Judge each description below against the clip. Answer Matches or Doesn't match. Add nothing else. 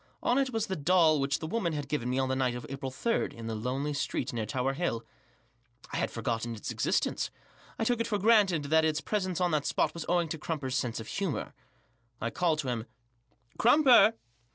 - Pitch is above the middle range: Doesn't match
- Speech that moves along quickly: Matches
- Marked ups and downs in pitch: Matches